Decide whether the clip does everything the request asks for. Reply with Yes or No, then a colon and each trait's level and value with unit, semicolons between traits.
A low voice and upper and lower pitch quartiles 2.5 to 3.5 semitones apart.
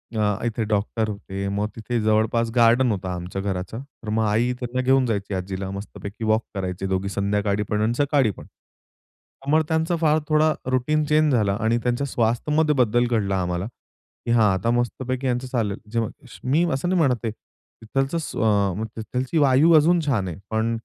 No: low, 115 Hz; average, 4.4 semitones